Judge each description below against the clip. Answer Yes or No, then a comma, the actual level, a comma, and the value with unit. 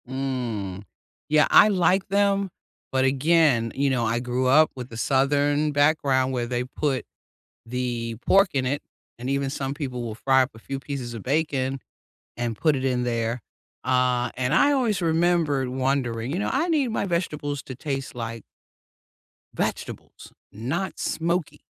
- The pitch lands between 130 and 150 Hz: Yes, low, 135 Hz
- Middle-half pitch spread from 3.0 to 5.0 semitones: Yes, average, 3.9 semitones